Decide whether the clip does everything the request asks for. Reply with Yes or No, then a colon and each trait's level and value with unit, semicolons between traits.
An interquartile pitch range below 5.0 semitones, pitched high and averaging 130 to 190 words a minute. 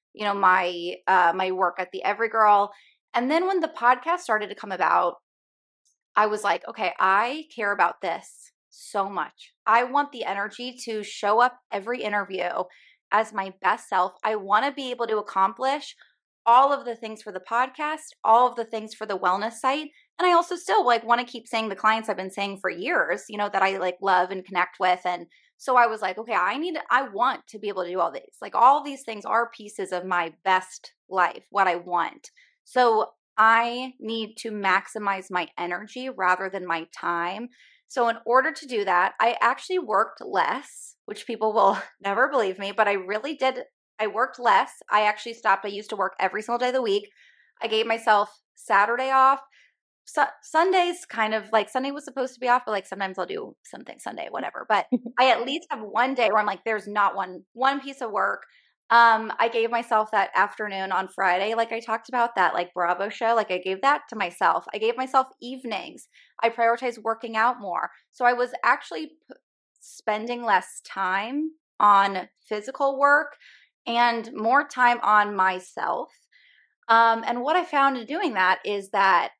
No: average, 4.3 semitones; high, 225 Hz; average, 200 wpm